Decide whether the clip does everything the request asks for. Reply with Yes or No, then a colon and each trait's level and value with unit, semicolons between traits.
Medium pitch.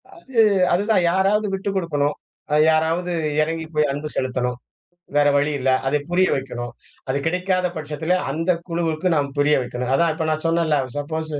Yes: medium, 160 Hz